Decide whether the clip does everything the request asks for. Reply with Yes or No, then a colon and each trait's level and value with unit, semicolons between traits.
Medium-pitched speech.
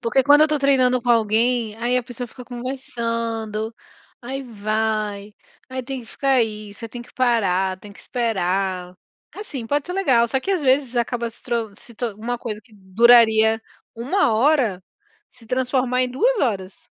No: high, 235 Hz